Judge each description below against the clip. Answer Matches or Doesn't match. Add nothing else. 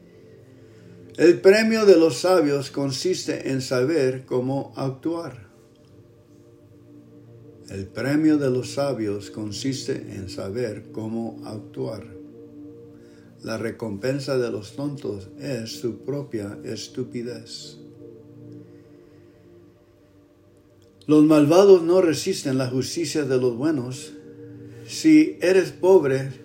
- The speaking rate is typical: Doesn't match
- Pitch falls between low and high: Doesn't match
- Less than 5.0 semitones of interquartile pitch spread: Doesn't match